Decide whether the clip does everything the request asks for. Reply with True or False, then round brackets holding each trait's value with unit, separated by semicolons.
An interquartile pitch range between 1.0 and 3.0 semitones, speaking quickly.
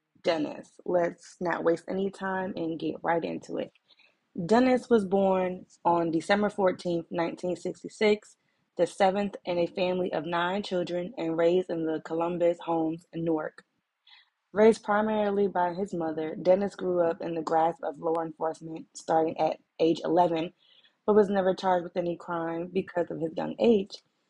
False (2.5 semitones; 160 wpm)